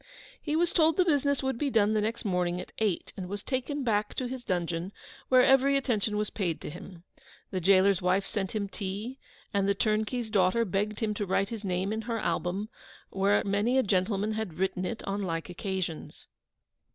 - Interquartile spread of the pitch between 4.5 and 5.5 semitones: No, average, 3.7 semitones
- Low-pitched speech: No, high, 205 Hz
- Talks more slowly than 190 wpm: No, average, 200 wpm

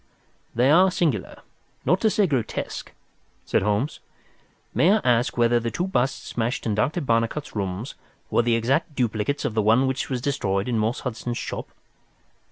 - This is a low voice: Yes, low, 120 Hz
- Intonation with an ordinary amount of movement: Yes, average, 4.0 semitones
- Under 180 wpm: Yes, average, 170 wpm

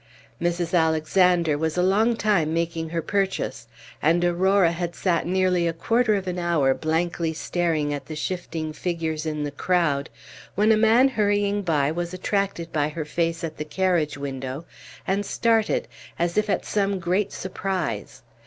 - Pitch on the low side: No, medium, 170 Hz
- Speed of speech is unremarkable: Yes, average, 160 wpm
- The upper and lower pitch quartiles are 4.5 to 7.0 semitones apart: No, average, 3.2 semitones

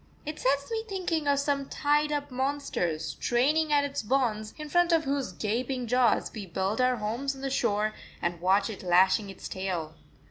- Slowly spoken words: No, average, 185 wpm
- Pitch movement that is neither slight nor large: No, wide, 5.7 semitones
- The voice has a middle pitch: No, very high, 255 Hz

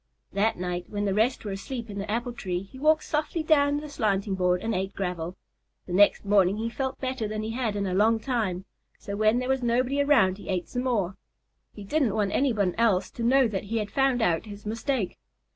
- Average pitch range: Yes, average, 4.5 semitones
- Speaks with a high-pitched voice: Yes, high, 215 Hz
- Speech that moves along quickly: Yes, fast, 225 wpm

